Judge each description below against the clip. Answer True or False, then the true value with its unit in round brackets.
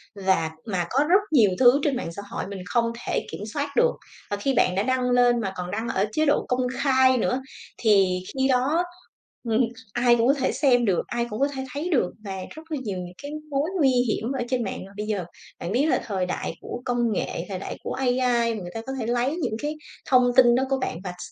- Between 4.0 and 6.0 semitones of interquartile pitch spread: True (4.6 semitones)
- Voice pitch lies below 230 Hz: False (245 Hz)